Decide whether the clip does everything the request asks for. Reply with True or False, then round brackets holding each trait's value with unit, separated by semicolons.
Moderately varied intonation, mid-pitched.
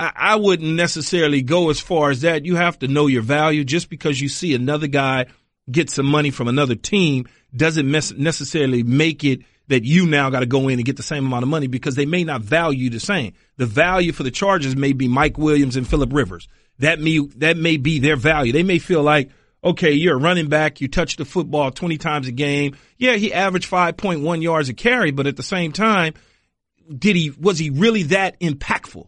True (3.6 semitones; 150 Hz)